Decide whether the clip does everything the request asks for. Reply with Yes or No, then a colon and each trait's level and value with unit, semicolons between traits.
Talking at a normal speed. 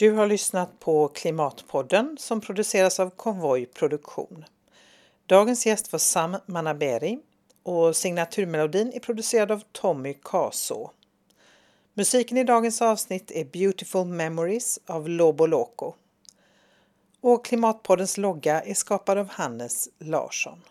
No: slow, 110 wpm